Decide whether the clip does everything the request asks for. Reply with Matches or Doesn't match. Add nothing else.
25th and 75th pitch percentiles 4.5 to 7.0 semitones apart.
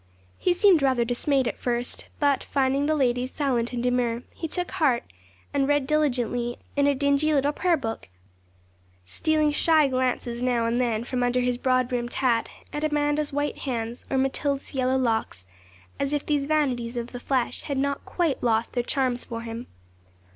Doesn't match